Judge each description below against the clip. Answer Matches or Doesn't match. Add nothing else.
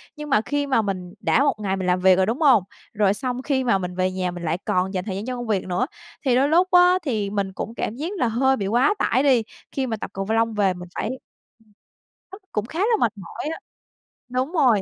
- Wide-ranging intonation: Matches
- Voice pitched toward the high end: Matches